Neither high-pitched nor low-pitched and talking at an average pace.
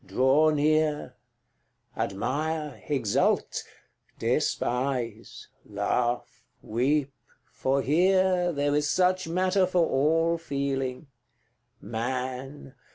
No: medium, 145 Hz; slow, 85 wpm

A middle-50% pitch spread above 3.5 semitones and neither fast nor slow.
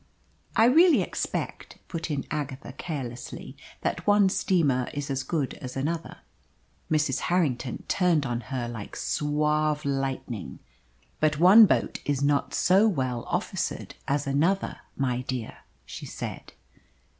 No: average, 4.2 semitones; slow, 130 wpm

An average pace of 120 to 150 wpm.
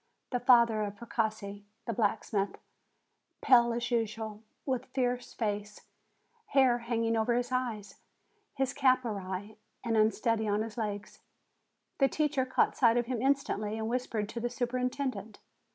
Yes: average, 140 wpm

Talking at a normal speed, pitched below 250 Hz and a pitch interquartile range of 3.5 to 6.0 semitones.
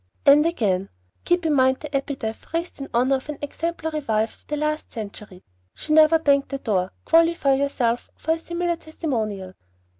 No: average, 175 wpm; very high, 280 Hz; wide, 5.5 semitones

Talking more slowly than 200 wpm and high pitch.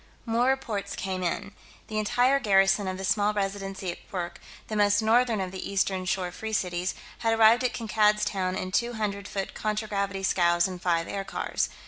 Yes: average, 180 wpm; high, 200 Hz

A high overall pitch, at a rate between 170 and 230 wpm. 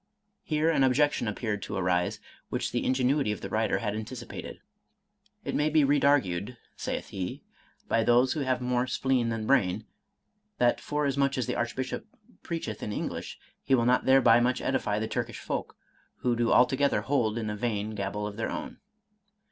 No: low, 120 Hz; average, 180 wpm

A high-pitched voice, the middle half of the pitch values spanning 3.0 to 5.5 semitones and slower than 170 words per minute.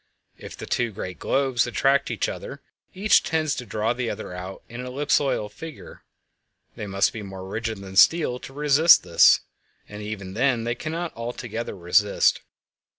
No: low, 120 Hz; average, 5.1 semitones; average, 155 wpm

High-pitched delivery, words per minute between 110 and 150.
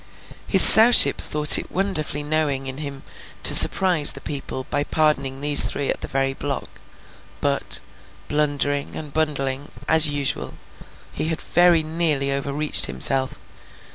No: medium, 145 Hz; average, 140 wpm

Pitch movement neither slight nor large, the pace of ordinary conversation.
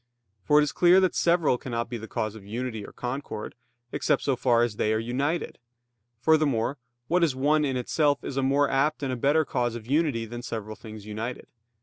No: average, 4.4 semitones; fast, 210 wpm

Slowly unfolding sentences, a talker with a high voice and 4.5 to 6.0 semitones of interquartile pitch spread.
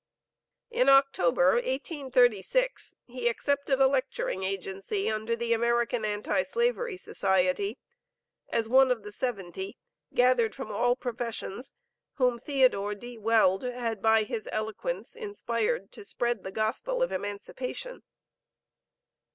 No: slow, 120 wpm; high, 240 Hz; average, 4.1 semitones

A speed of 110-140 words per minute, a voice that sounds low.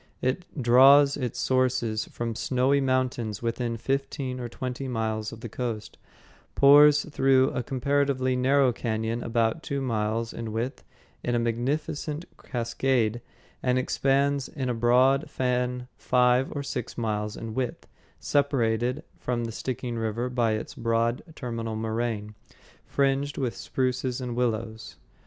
Yes: slow, 135 wpm; low, 125 Hz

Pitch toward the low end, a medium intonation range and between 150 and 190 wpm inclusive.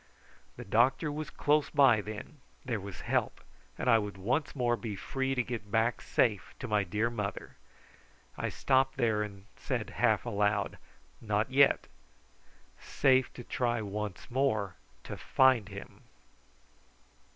No: low, 115 Hz; average, 4.1 semitones; average, 140 wpm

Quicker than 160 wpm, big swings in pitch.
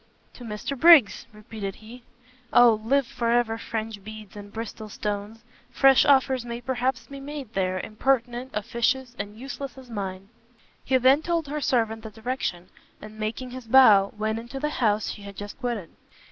No: average, 170 wpm; average, 3.5 semitones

